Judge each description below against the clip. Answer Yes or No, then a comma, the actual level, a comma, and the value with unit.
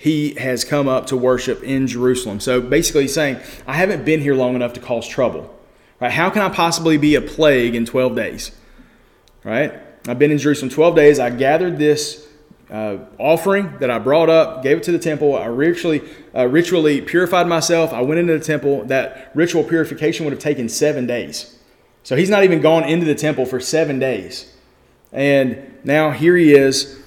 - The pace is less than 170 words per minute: No, average, 195 wpm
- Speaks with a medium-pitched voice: Yes, medium, 150 Hz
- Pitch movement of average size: Yes, average, 3.9 semitones